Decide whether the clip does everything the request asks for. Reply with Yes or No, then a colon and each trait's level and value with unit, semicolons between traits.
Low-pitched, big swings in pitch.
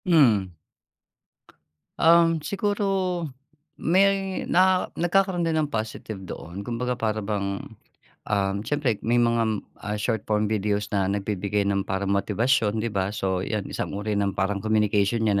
Yes: low, 110 Hz; wide, 7.5 semitones